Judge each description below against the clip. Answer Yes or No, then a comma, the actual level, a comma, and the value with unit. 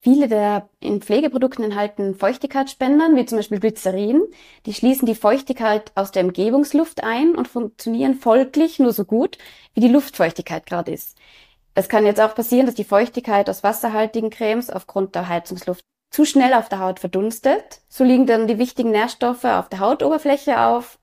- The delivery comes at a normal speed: Yes, average, 170 wpm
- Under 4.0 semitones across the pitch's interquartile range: No, average, 4.3 semitones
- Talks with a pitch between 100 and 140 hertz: No, high, 225 Hz